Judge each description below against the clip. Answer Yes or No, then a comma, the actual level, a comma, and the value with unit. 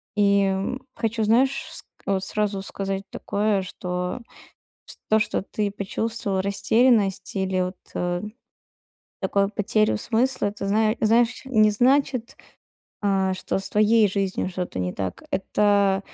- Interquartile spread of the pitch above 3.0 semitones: No, narrow, 2.4 semitones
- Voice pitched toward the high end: Yes, high, 200 Hz